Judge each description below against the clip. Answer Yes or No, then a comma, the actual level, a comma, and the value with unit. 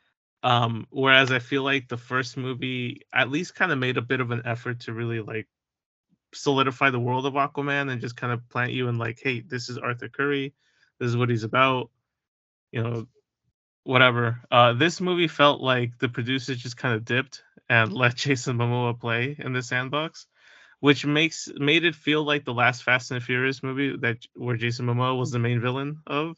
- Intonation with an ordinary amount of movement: No, narrow, 2.3 semitones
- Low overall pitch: Yes, low, 130 Hz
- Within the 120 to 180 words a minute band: No, average, 200 wpm